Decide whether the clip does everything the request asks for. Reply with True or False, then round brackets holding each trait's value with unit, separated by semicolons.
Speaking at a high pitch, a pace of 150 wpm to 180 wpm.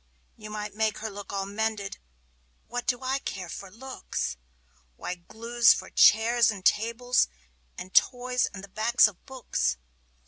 True (215 Hz; 160 wpm)